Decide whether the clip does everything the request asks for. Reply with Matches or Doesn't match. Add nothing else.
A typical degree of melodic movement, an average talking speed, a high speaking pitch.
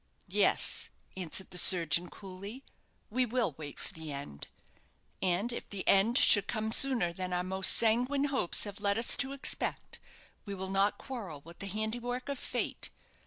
Matches